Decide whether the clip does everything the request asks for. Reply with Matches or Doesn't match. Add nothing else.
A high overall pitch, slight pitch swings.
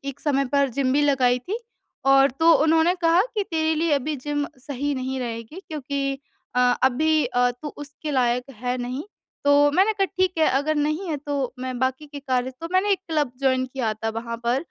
Doesn't match